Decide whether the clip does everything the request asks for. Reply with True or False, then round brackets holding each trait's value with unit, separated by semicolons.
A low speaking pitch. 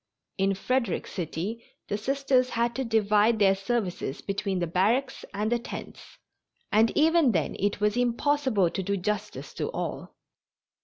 False (215 Hz)